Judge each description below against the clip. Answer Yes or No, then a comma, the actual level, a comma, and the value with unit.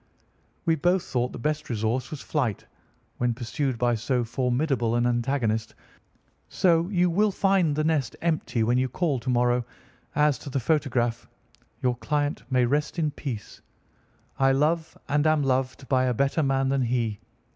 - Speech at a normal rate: Yes, average, 165 wpm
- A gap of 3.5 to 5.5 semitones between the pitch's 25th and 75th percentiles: Yes, average, 3.9 semitones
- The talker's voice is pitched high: No, low, 135 Hz